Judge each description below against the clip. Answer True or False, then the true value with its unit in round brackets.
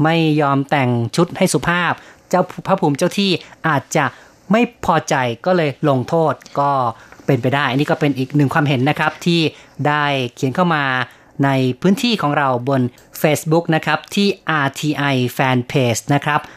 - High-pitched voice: False (150 Hz)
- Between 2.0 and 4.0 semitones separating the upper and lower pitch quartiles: True (3.4 semitones)